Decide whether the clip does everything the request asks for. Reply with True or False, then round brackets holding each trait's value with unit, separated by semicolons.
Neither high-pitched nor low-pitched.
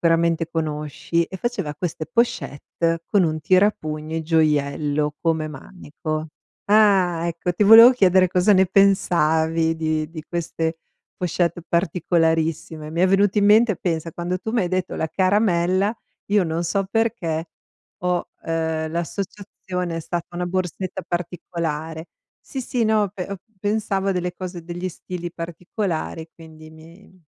True (175 Hz)